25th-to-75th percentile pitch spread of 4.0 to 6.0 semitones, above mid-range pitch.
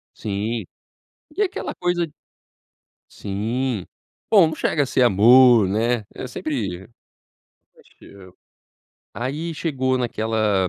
No: wide, 5.5 semitones; low, 120 Hz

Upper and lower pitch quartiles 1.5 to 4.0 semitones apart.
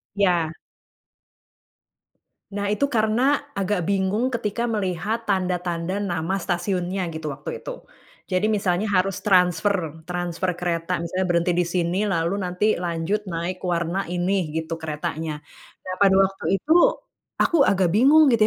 Yes: average, 2.8 semitones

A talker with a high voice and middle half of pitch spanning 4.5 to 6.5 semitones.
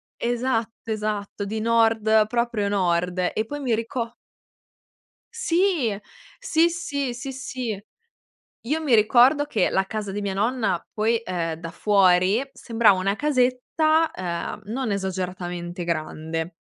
Yes: high, 220 Hz; average, 4.9 semitones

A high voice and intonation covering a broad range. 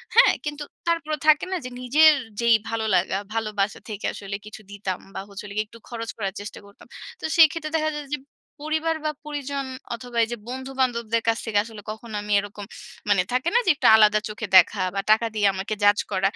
Yes: high, 230 Hz; wide, 5.9 semitones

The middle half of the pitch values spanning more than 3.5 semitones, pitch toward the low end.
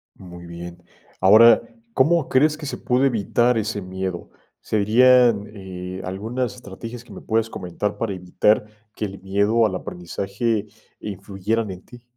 Yes: average, 3.9 semitones; low, 105 Hz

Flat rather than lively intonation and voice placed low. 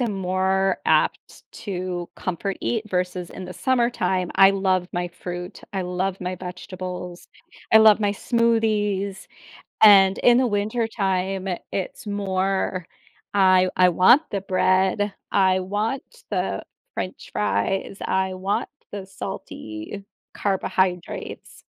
No: narrow, 1.9 semitones; high, 190 Hz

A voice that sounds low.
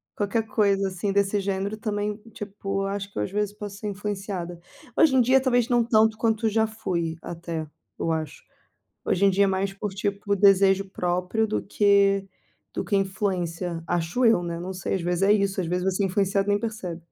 No: high, 195 Hz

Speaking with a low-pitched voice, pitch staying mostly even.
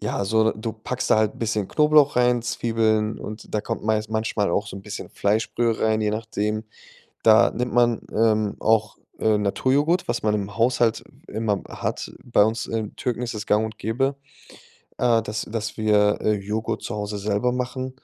Yes: low, 110 Hz; narrow, 1.9 semitones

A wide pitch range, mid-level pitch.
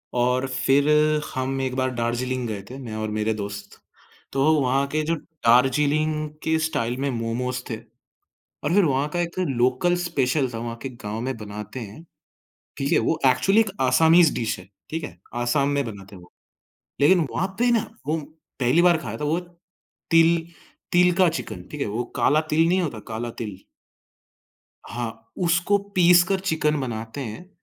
No: wide, 5.7 semitones; low, 130 Hz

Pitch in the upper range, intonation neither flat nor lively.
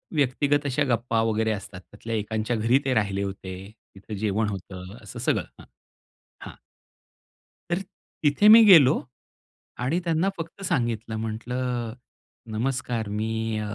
No: low, 115 Hz; average, 3.9 semitones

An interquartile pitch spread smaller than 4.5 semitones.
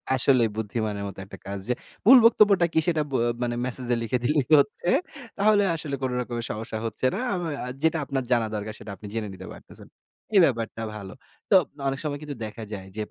No: wide, 5.6 semitones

